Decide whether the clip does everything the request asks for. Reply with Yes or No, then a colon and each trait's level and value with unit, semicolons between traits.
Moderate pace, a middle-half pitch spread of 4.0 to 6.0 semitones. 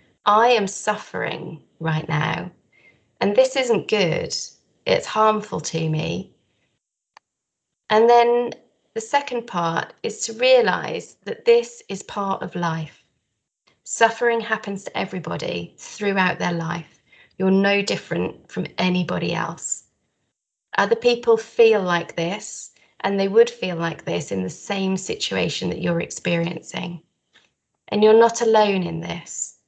No: slow, 130 wpm; average, 5.3 semitones